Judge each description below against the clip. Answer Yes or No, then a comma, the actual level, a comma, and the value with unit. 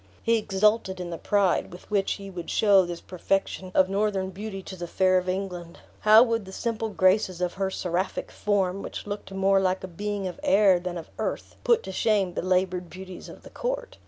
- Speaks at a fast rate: Yes, fast, 210 wpm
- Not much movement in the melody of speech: Yes, narrow, 2.1 semitones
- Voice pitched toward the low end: No, high, 190 Hz